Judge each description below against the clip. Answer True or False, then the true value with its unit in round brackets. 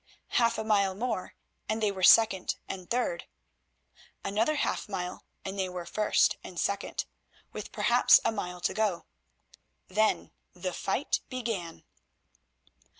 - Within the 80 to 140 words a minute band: True (135 wpm)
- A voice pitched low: False (200 Hz)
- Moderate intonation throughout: True (3.4 semitones)